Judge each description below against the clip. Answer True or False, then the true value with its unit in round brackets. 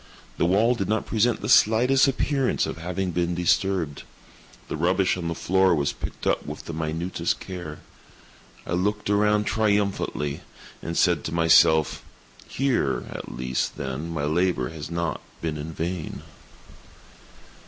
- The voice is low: True (85 Hz)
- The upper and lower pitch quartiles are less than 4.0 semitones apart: False (4.4 semitones)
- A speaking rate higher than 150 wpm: False (145 wpm)